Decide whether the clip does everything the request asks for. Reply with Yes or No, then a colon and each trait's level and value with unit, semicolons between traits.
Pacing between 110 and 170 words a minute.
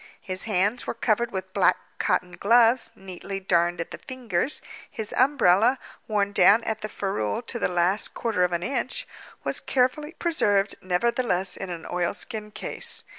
Yes: average, 160 wpm